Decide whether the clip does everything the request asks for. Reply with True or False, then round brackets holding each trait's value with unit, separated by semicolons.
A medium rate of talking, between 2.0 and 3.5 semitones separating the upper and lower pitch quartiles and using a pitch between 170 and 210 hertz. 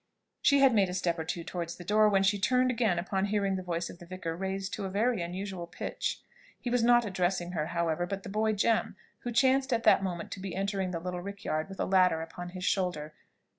False (240 wpm; 3.2 semitones; 190 Hz)